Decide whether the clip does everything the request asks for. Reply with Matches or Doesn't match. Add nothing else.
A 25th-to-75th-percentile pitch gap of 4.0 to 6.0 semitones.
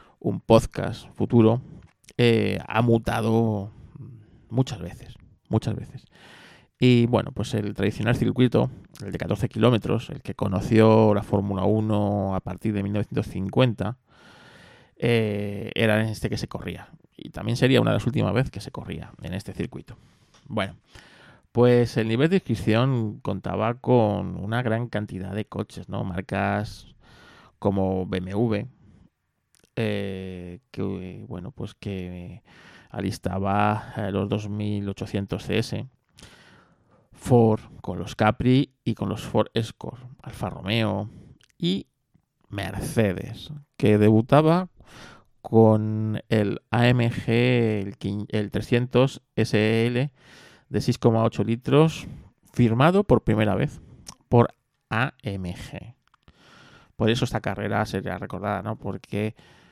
Doesn't match